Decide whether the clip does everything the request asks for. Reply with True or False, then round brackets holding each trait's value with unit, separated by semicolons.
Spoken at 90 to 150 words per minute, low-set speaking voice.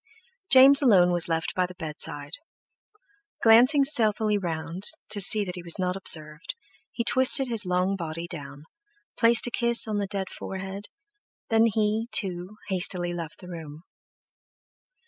False (145 wpm; 190 Hz)